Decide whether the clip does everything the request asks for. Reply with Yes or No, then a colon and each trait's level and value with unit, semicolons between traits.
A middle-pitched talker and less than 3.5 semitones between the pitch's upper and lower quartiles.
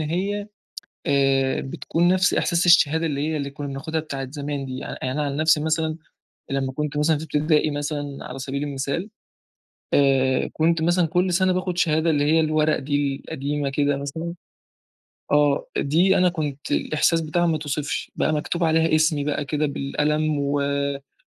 Yes: medium, 150 Hz; narrow, 2.4 semitones